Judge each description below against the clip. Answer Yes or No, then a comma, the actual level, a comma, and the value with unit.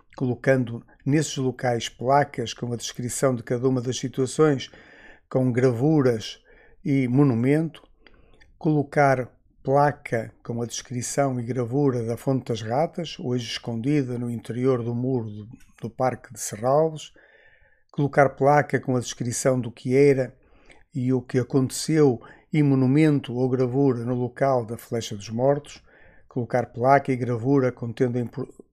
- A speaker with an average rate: Yes, average, 140 wpm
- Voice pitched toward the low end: Yes, low, 130 Hz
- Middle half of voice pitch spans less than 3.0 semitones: Yes, narrow, 2.5 semitones